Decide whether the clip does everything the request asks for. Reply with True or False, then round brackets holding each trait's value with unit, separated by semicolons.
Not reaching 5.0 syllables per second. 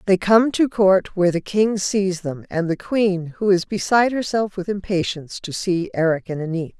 False (5.1 syllables/s)